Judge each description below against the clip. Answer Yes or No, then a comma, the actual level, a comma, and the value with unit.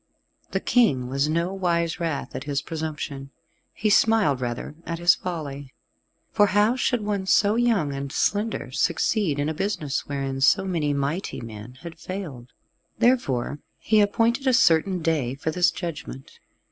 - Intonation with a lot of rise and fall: Yes, wide, 6.4 semitones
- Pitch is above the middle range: No, medium, 165 Hz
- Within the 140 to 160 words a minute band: Yes, average, 155 wpm